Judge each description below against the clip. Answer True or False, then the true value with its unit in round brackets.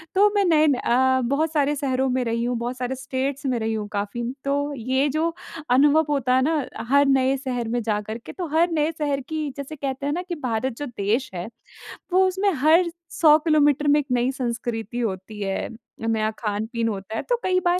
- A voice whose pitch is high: True (265 Hz)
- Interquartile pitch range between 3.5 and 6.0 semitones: True (4.1 semitones)